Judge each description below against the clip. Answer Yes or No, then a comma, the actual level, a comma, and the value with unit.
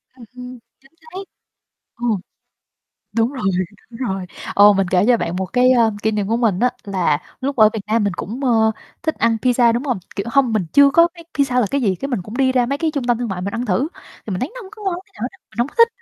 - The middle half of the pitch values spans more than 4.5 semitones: No, average, 4.2 semitones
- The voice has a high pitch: Yes, high, 240 Hz